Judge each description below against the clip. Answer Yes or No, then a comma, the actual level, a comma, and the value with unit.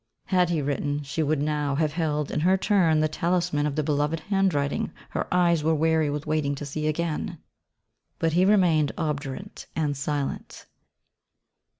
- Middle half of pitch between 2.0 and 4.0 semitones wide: Yes, narrow, 2.6 semitones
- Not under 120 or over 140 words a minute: No, average, 165 wpm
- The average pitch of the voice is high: No, medium, 155 Hz